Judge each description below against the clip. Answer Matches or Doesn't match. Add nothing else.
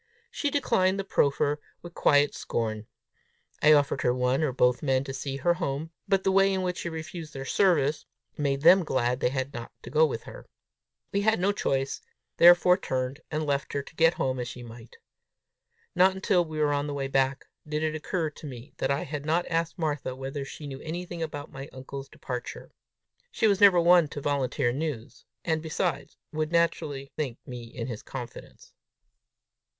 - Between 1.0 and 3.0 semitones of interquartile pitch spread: Doesn't match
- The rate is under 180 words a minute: Doesn't match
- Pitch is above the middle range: Doesn't match